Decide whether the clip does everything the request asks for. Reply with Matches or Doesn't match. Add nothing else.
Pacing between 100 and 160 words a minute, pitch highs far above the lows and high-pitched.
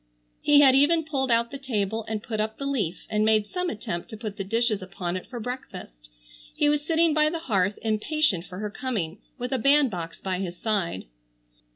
Doesn't match